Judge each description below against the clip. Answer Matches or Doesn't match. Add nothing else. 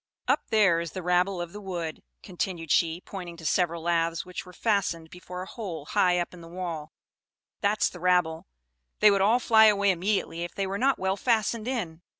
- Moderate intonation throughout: Matches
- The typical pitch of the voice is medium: Matches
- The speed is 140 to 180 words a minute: Doesn't match